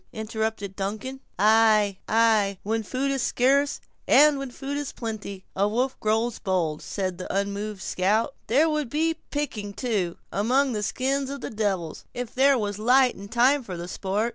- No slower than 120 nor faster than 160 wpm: No, average, 170 wpm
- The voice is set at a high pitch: Yes, high, 220 Hz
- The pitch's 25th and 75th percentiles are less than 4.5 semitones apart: No, average, 4.8 semitones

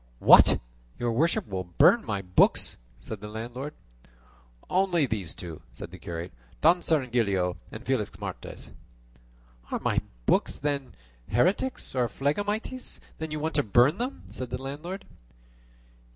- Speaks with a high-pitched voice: No, low, 130 Hz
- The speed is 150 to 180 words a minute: No, slow, 135 wpm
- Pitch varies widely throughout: Yes, wide, 7.6 semitones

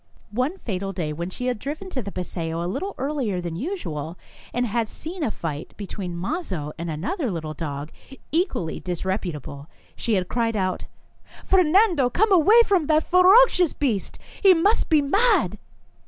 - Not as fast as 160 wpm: No, average, 165 wpm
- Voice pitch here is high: Yes, high, 230 Hz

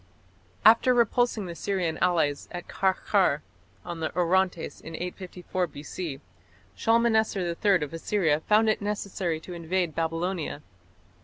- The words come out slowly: Yes, slow, 125 wpm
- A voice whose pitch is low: No, medium, 180 Hz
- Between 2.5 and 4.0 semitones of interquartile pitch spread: Yes, average, 3.6 semitones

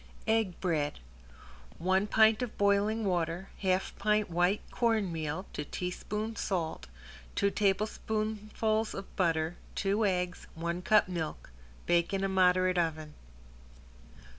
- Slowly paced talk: Yes, slow, 115 wpm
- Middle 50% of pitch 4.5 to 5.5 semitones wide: No, average, 3.6 semitones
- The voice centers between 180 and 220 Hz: Yes, high, 190 Hz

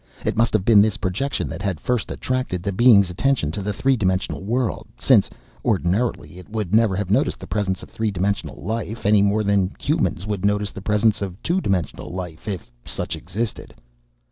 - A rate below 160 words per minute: No, average, 195 wpm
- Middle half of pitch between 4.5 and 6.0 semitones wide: No, average, 3.1 semitones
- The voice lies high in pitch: No, low, 100 Hz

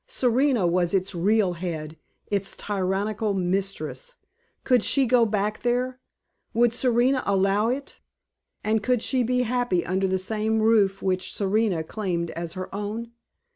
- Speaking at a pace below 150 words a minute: Yes, average, 140 wpm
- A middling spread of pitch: Yes, average, 4.2 semitones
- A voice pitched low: No, high, 210 Hz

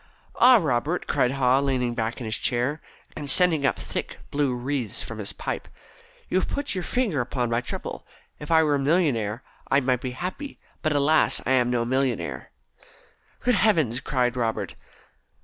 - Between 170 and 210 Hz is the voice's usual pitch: No, low, 135 Hz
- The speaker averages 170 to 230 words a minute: Yes, average, 175 wpm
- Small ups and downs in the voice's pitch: No, average, 4.3 semitones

